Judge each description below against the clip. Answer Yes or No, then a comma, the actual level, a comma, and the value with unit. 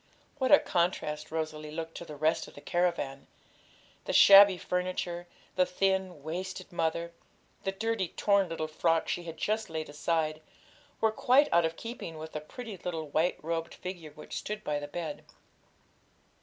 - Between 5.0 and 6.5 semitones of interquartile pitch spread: No, average, 3.2 semitones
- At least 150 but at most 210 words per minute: Yes, average, 165 wpm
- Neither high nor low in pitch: Yes, medium, 170 Hz